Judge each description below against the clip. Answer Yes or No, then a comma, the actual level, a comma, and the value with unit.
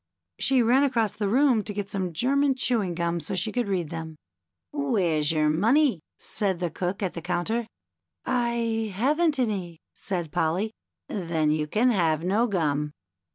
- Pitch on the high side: Yes, high, 200 Hz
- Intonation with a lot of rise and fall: Yes, wide, 5.9 semitones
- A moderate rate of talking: Yes, average, 175 wpm